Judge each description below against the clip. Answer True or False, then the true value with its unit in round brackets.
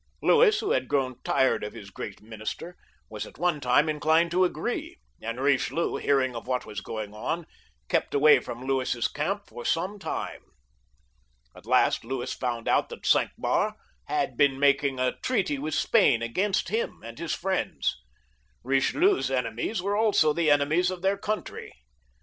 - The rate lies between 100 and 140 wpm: False (165 wpm)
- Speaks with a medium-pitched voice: True (145 Hz)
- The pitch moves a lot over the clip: True (6.5 semitones)